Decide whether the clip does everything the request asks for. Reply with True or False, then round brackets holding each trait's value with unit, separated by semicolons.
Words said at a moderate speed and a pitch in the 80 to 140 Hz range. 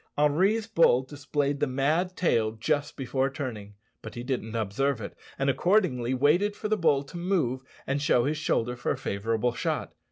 True (180 wpm; 135 Hz)